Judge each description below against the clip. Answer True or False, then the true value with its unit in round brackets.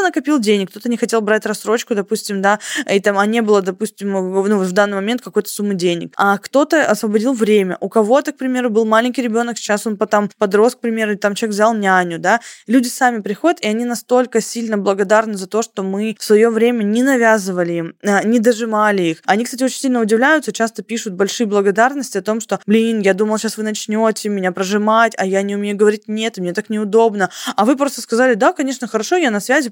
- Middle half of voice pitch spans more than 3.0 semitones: False (2.5 semitones)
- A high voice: True (220 Hz)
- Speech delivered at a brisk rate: True (215 wpm)